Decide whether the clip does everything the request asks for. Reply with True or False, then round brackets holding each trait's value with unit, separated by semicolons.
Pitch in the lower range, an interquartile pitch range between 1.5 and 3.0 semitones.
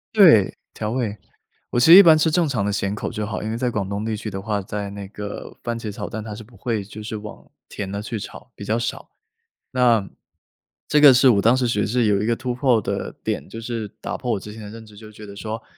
True (110 Hz; 2.7 semitones)